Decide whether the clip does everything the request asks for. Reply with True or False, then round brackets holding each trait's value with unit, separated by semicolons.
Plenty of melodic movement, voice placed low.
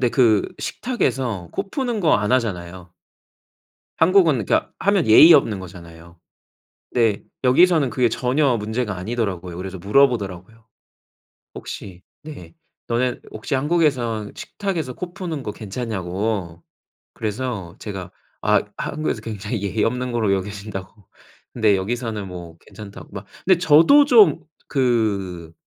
True (6.1 semitones; 115 Hz)